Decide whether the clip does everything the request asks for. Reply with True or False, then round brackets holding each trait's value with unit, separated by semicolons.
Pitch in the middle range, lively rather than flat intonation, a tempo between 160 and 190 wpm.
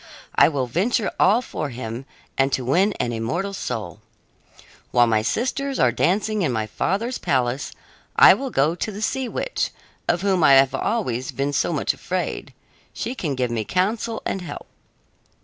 True (170 Hz; 9.0 semitones; 170 wpm)